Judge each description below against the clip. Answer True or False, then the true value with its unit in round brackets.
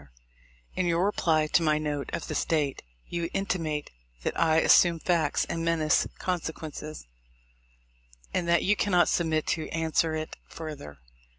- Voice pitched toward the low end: False (160 Hz)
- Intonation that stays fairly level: True (1.9 semitones)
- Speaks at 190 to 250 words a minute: False (155 wpm)